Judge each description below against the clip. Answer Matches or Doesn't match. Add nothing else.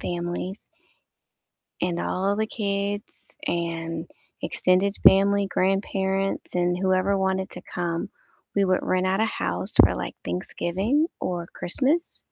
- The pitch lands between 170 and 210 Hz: Matches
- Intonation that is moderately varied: Doesn't match